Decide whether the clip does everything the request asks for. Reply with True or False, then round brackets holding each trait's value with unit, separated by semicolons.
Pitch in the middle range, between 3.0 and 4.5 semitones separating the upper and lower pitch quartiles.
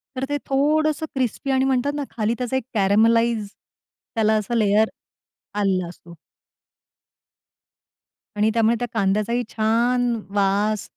False (230 Hz; 3.3 semitones)